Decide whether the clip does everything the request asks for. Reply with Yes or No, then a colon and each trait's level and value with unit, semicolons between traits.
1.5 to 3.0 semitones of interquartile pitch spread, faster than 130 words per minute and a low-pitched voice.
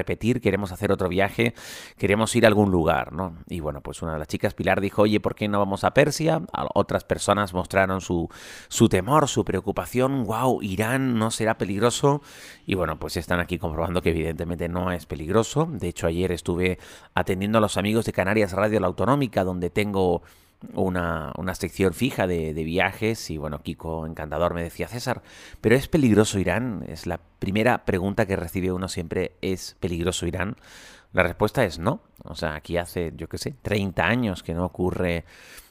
No: average, 3.8 semitones; fast, 190 wpm; very low, 95 Hz